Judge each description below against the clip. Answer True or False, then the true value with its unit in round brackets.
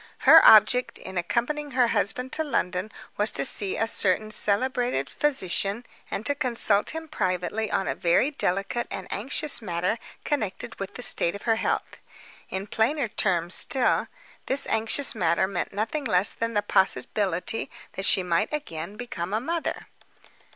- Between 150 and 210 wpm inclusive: True (160 wpm)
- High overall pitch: True (215 Hz)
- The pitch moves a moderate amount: True (4.9 semitones)